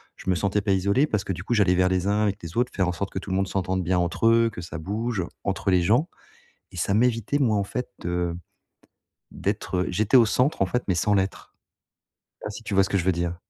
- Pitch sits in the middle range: No, very low, 95 Hz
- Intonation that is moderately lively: Yes, average, 3.3 semitones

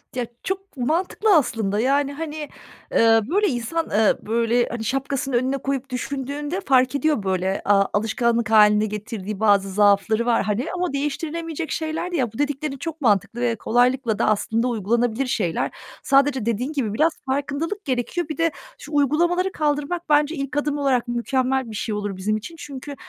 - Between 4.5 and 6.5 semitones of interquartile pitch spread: Yes, average, 4.9 semitones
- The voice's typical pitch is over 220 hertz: Yes, very high, 260 Hz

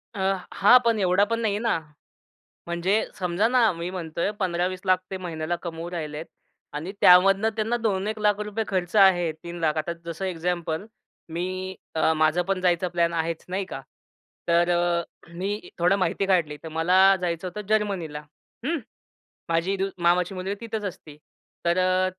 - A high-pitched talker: No, medium, 180 Hz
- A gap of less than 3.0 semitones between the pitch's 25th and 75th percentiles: Yes, narrow, 2.6 semitones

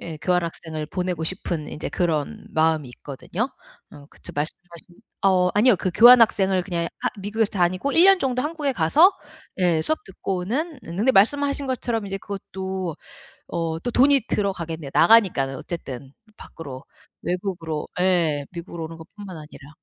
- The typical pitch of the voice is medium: Yes, medium, 180 Hz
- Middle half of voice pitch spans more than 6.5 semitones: No, average, 5.2 semitones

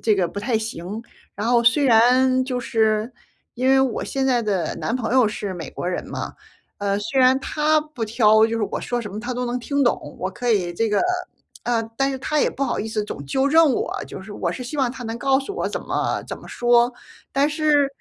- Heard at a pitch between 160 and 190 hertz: No, high, 240 Hz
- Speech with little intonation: No, average, 3.8 semitones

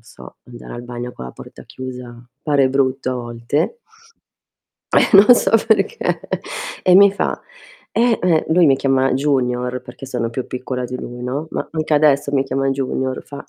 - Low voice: Yes, low, 130 Hz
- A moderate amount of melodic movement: Yes, average, 3.2 semitones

